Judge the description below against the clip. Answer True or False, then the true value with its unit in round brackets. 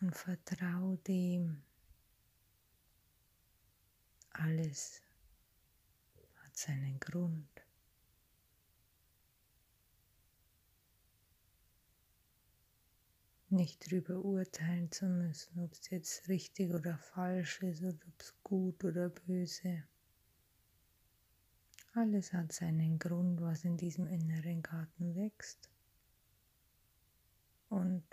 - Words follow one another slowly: True (75 wpm)